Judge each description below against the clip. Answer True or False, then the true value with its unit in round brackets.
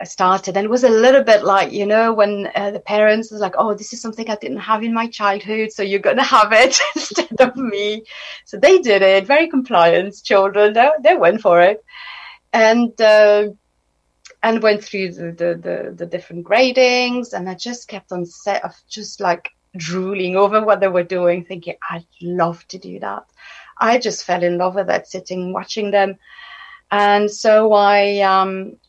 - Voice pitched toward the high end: True (205 Hz)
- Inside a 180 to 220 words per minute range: True (190 wpm)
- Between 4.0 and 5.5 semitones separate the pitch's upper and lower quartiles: False (3.2 semitones)